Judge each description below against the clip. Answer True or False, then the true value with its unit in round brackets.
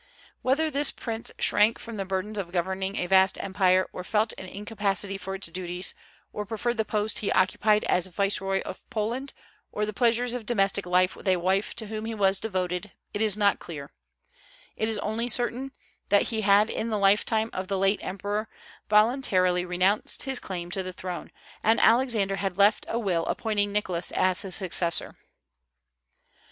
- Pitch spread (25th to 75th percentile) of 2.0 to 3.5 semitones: True (2.8 semitones)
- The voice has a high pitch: True (200 Hz)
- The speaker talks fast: False (180 wpm)